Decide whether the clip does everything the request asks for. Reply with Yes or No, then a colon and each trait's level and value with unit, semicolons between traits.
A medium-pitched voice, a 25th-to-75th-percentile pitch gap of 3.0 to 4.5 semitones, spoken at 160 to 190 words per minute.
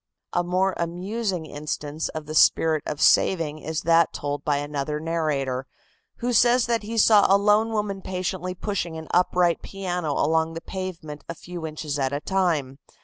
Yes: medium, 170 Hz; average, 4.0 semitones; average, 170 wpm